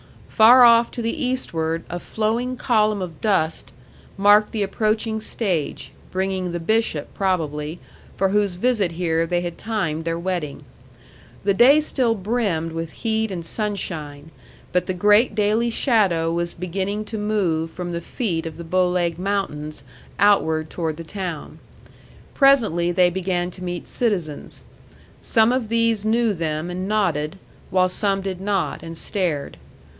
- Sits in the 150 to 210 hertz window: Yes, high, 190 Hz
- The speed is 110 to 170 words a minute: Yes, average, 150 wpm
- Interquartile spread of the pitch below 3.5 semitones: No, average, 4.4 semitones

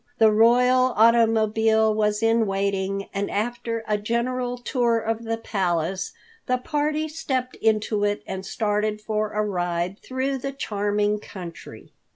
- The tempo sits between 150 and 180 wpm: No, average, 140 wpm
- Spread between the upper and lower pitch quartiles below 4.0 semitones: Yes, average, 2.7 semitones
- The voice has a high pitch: Yes, high, 220 Hz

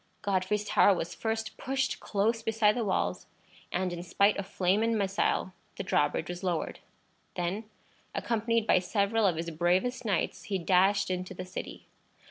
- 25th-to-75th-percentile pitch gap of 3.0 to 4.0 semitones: Yes, average, 3.5 semitones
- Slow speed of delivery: No, average, 160 wpm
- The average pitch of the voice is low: No, high, 195 Hz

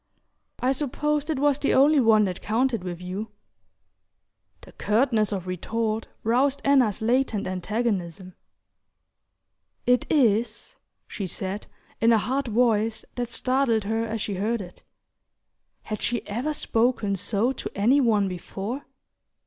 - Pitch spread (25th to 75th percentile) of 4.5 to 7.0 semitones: No, average, 4.0 semitones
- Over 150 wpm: No, slow, 135 wpm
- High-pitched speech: Yes, high, 225 Hz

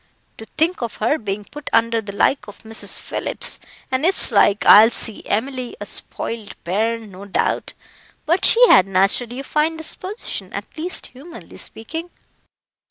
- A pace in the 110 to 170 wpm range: Yes, average, 160 wpm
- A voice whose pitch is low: No, high, 230 Hz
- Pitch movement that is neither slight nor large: No, wide, 6.7 semitones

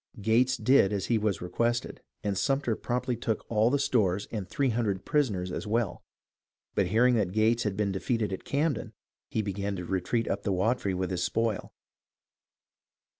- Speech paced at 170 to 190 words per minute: Yes, average, 175 wpm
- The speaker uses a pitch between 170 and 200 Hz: No, low, 110 Hz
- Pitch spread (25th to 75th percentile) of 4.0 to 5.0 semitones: No, average, 3.6 semitones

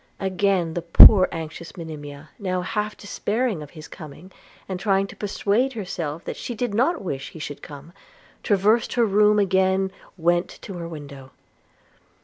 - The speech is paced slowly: No, average, 155 wpm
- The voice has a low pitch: No, medium, 185 Hz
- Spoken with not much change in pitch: No, average, 4.3 semitones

